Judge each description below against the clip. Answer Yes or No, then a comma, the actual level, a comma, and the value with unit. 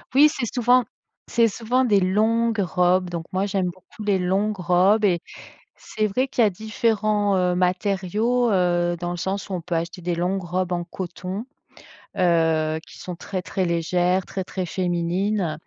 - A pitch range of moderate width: Yes, average, 3.1 semitones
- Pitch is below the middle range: No, medium, 185 Hz